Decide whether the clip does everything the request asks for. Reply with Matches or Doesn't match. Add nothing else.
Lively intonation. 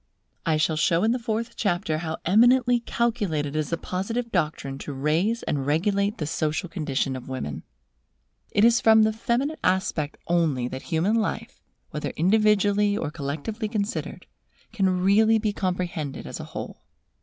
Matches